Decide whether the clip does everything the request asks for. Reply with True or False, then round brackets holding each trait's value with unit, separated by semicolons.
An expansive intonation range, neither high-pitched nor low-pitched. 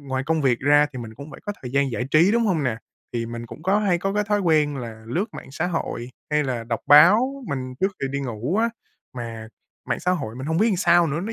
True (6.8 semitones; 145 Hz)